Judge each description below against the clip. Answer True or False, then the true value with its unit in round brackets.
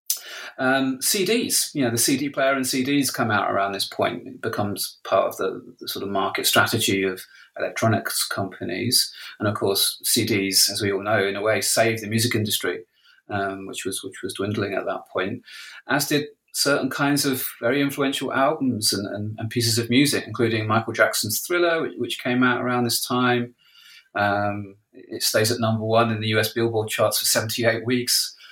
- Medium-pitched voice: False (115 Hz)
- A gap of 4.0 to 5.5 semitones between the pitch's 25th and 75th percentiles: False (3.4 semitones)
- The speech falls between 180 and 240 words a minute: True (190 wpm)